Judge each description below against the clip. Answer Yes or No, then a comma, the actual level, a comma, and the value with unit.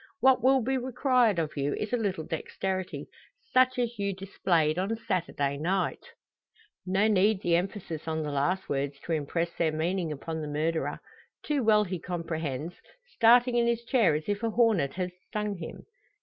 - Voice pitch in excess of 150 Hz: Yes, medium, 185 Hz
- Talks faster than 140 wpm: Yes, average, 175 wpm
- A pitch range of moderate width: No, wide, 5.9 semitones